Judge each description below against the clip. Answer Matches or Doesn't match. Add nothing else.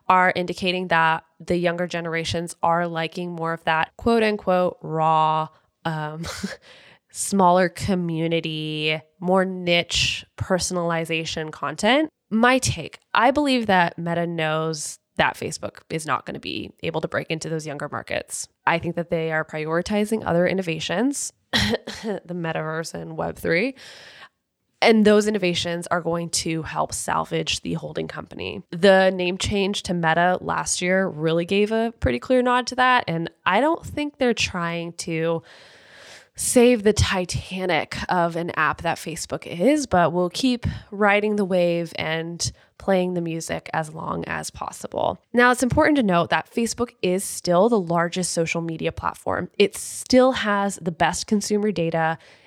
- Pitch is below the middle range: Doesn't match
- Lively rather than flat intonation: Doesn't match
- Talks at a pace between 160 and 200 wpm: Doesn't match